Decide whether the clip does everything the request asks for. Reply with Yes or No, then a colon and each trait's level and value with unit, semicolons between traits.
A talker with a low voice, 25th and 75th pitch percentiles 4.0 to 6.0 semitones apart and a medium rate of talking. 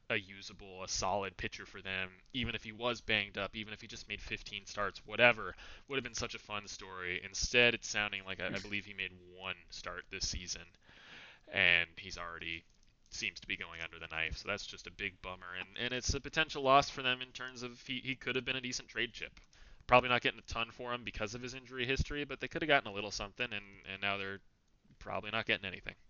No: low, 105 Hz; average, 4.4 semitones; fast, 240 wpm